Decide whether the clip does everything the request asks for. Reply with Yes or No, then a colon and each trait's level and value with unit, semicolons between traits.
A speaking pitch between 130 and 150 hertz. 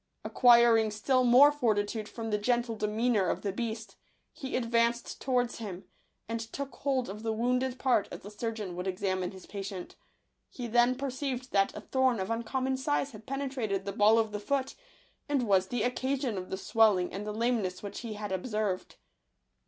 No: high, 225 Hz